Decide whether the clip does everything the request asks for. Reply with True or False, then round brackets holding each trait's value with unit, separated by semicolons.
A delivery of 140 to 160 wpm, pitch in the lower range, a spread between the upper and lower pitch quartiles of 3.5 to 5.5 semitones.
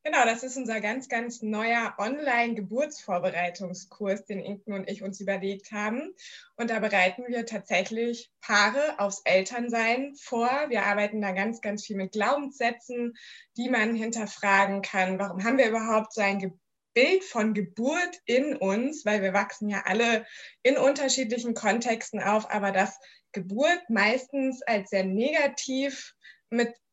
False (145 wpm; 225 Hz; 3.8 semitones)